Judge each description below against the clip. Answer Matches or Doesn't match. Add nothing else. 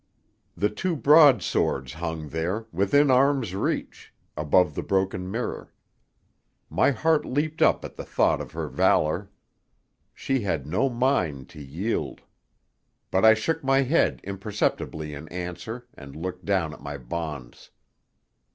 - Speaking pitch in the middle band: Doesn't match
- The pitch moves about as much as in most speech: Doesn't match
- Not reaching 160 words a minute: Matches